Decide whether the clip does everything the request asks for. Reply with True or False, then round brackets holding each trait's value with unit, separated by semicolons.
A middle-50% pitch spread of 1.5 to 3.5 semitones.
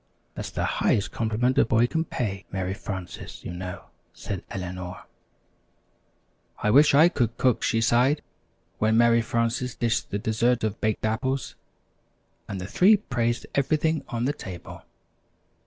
False (4.0 semitones)